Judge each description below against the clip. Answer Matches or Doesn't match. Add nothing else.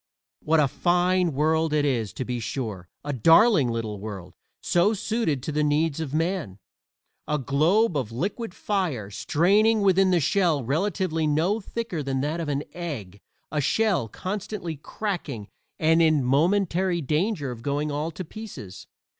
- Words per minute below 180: Matches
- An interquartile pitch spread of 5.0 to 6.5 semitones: Matches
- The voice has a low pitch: Doesn't match